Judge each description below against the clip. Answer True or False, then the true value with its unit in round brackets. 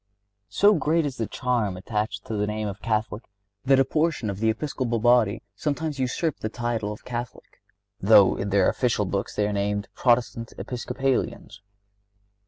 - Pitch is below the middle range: True (115 Hz)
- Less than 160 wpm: False (165 wpm)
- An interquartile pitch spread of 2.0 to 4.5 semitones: True (3.8 semitones)